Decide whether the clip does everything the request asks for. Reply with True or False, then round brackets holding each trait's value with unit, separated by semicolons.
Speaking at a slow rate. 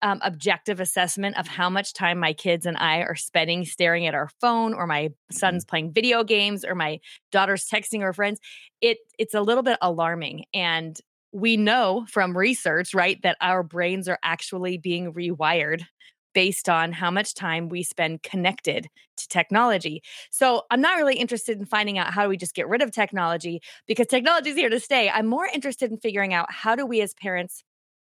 False (195 wpm)